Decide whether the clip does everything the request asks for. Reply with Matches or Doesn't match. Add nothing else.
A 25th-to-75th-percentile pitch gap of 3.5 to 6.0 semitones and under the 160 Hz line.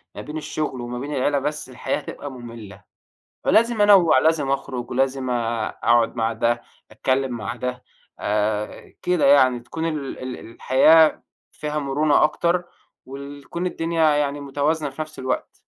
Matches